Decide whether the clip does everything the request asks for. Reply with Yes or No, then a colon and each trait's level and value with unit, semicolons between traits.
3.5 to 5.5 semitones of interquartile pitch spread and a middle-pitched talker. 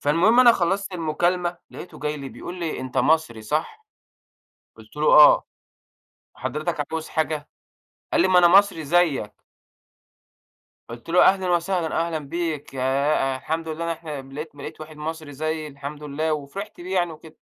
No: average, 3.0 semitones; medium, 160 Hz